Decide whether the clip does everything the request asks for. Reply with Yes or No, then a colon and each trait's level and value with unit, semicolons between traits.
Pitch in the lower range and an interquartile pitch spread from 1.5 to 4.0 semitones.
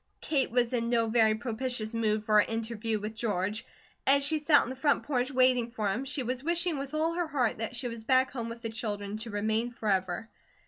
No: high, 235 Hz; average, 3.2 semitones